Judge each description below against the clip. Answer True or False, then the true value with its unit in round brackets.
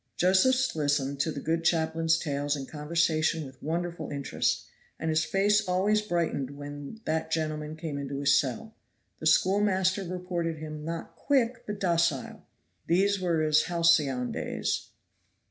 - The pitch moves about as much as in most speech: True (3.6 semitones)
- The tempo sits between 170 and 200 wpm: False (145 wpm)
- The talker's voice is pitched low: False (165 Hz)